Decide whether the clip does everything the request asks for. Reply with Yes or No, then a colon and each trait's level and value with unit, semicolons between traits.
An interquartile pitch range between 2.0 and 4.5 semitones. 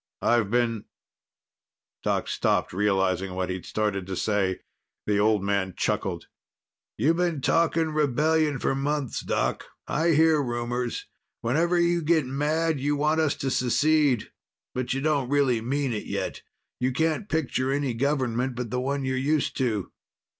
No: average, 4.9 semitones